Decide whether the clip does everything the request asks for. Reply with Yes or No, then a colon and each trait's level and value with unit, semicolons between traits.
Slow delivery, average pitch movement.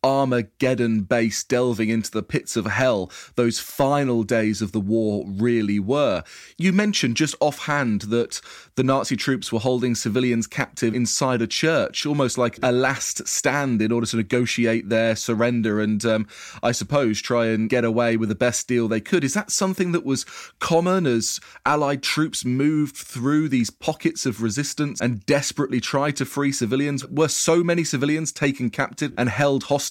No: average, 175 wpm; average, 3.9 semitones